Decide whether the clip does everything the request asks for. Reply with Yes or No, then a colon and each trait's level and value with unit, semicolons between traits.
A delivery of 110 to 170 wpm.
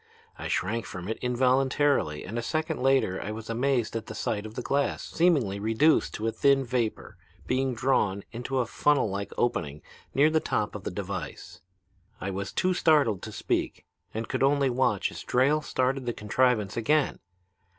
No: average, 180 wpm